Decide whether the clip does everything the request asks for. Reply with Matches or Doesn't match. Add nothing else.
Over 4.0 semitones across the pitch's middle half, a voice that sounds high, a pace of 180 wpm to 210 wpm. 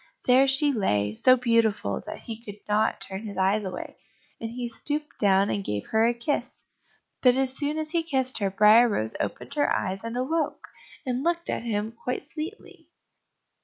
Matches